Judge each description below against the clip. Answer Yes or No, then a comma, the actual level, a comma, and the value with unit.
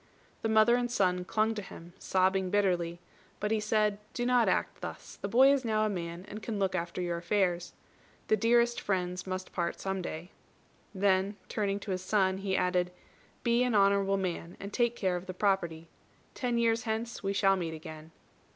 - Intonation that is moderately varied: Yes, average, 3.2 semitones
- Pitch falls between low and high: No, high, 195 Hz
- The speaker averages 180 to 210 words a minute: Yes, average, 190 wpm